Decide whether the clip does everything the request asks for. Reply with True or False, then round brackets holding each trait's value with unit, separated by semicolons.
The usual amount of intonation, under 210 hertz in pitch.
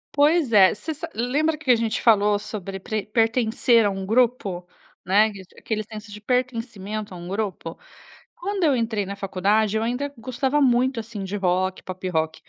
False (4.1 semitones; 220 Hz)